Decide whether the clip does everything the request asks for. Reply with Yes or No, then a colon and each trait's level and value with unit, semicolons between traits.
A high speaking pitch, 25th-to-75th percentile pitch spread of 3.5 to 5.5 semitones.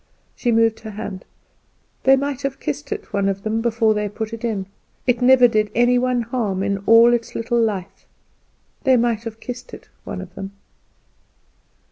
No: high, 225 Hz; average, 3.0 semitones